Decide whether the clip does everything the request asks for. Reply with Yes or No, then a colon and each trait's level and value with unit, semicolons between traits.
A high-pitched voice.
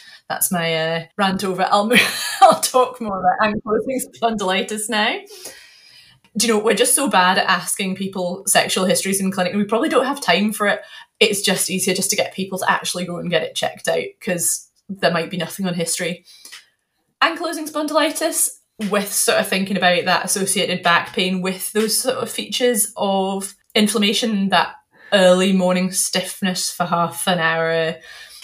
Yes: high, 195 Hz